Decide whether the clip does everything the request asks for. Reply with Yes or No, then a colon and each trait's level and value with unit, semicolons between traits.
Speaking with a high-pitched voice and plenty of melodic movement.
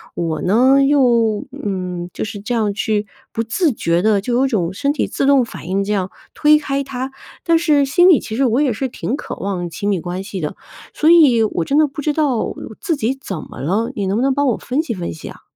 Yes: high, 230 Hz; wide, 5.8 semitones